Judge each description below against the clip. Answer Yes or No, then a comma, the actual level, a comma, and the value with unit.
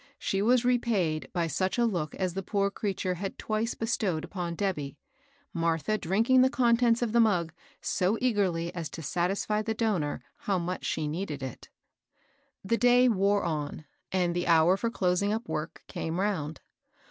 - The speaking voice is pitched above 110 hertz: Yes, high, 190 Hz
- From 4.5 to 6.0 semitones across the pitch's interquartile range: Yes, average, 4.8 semitones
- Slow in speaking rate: No, average, 170 wpm